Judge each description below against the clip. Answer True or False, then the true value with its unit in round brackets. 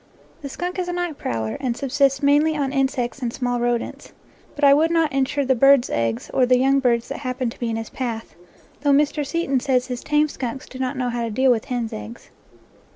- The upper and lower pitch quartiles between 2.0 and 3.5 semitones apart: True (2.8 semitones)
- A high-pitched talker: True (265 Hz)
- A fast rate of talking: True (230 wpm)